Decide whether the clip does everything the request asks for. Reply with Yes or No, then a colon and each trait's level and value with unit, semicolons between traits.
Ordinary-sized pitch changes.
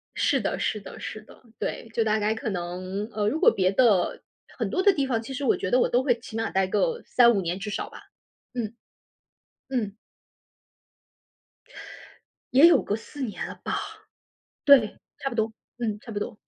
Yes: average, 3.6 semitones